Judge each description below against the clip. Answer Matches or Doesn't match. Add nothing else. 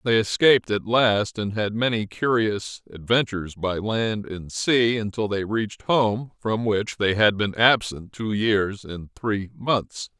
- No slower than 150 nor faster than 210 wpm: Matches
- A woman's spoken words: Doesn't match